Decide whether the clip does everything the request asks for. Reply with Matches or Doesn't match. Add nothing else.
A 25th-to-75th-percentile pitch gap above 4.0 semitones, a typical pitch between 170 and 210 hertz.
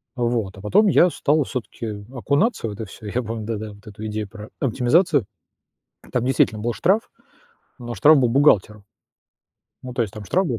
Doesn't match